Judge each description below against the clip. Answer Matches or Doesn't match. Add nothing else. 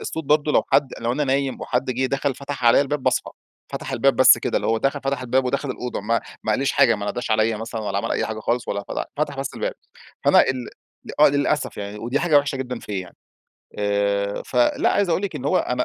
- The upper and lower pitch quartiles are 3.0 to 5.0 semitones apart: Matches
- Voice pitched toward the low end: Matches